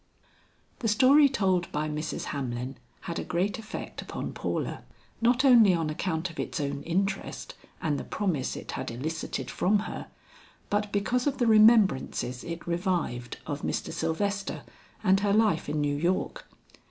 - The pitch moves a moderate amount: No, wide, 5.8 semitones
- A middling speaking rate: Yes, average, 155 wpm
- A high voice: No, medium, 180 Hz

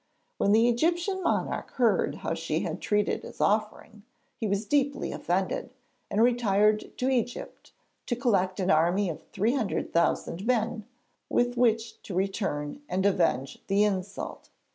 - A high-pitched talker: Yes, high, 215 Hz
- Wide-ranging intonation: No, average, 3.9 semitones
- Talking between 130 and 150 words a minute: Yes, average, 145 wpm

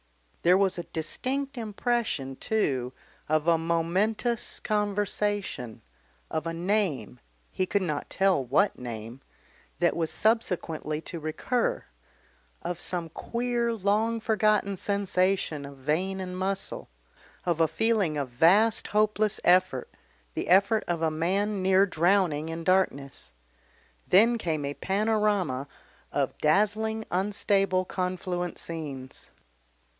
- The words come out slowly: Yes, slow, 120 wpm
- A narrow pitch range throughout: No, average, 4.7 semitones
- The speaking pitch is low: No, medium, 185 Hz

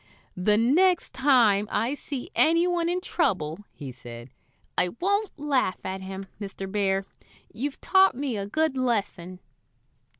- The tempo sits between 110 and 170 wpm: Yes, average, 140 wpm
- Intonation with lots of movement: Yes, wide, 8.3 semitones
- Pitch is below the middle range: No, high, 230 Hz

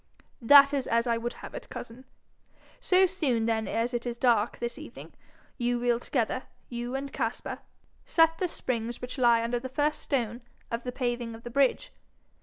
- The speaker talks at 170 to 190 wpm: Yes, average, 185 wpm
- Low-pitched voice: No, high, 245 Hz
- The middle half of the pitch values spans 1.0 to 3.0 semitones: Yes, narrow, 2.5 semitones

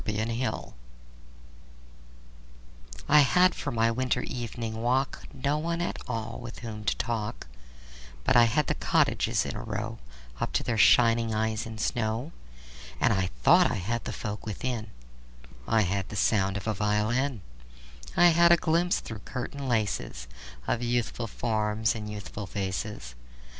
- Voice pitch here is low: Yes, low, 115 Hz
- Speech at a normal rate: Yes, average, 155 wpm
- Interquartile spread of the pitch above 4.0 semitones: No, average, 2.7 semitones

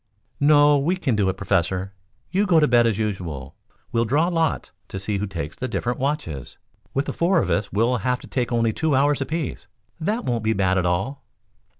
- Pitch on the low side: Yes, low, 120 Hz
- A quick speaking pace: Yes, fast, 210 wpm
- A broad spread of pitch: Yes, wide, 7.0 semitones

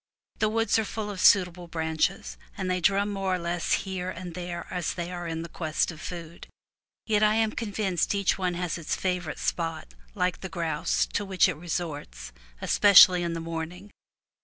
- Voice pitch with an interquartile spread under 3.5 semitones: Yes, average, 2.7 semitones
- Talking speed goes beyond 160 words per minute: Yes, average, 185 wpm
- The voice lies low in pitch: No, medium, 180 Hz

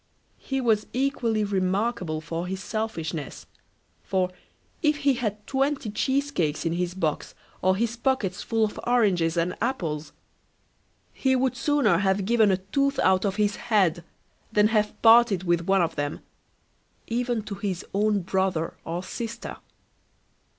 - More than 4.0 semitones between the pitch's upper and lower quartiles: Yes, average, 4.7 semitones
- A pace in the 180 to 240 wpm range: No, average, 145 wpm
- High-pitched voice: Yes, high, 205 Hz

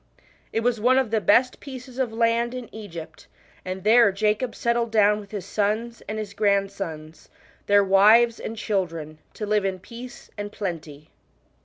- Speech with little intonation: No, average, 3.1 semitones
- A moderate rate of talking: Yes, average, 165 wpm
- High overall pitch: Yes, high, 210 Hz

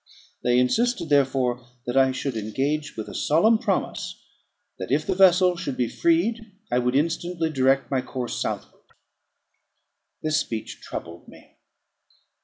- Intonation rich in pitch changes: Yes, wide, 6.0 semitones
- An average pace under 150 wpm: Yes, average, 140 wpm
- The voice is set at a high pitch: No, medium, 140 Hz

